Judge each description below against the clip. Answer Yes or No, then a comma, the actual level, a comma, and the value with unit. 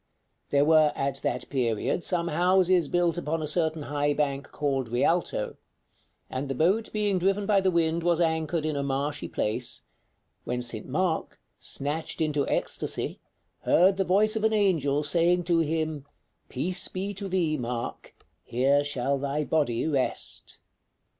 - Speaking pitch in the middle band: Yes, medium, 155 Hz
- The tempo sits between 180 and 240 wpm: No, average, 155 wpm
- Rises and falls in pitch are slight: No, average, 4.1 semitones